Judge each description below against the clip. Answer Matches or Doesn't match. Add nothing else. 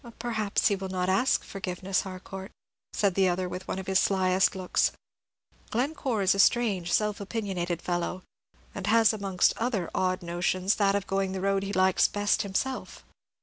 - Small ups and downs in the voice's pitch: Matches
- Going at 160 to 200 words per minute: Matches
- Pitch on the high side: Matches